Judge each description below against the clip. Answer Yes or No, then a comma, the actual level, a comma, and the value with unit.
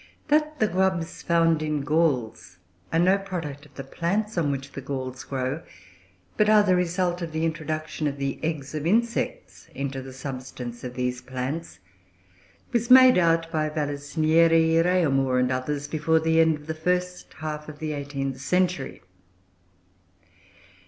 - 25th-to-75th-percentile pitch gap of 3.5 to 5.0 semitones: Yes, average, 3.9 semitones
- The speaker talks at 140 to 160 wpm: Yes, average, 155 wpm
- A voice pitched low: No, medium, 155 Hz